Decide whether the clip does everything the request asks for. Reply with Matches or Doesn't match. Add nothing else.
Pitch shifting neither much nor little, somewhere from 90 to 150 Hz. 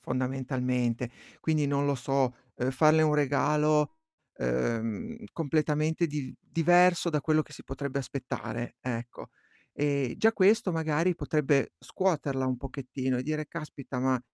Matches